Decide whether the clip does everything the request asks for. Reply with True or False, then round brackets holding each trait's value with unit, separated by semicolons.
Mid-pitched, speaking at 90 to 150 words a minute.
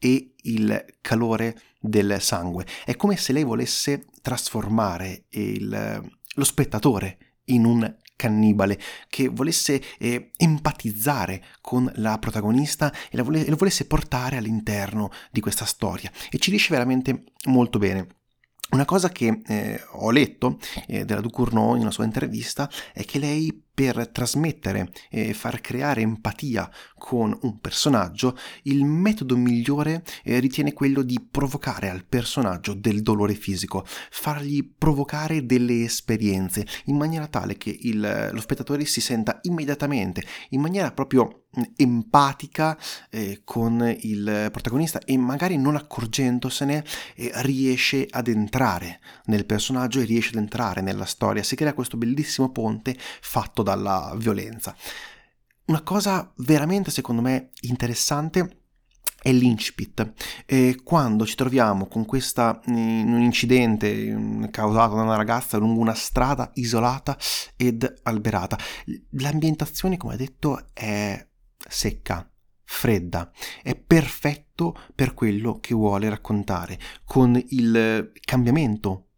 False (120 Hz; 125 wpm)